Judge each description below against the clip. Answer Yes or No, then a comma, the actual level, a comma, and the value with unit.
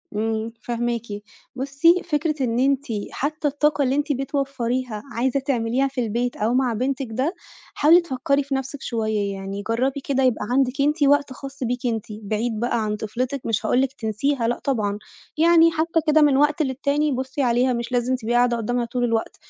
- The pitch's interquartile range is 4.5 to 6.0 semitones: No, average, 3.2 semitones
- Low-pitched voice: No, very high, 255 Hz